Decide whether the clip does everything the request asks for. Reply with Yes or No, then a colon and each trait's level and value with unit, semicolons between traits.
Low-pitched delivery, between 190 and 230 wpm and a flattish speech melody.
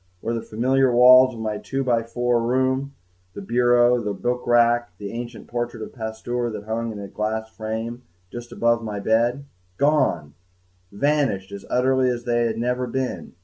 Yes: low, 120 Hz; average, 195 wpm; narrow, 2.0 semitones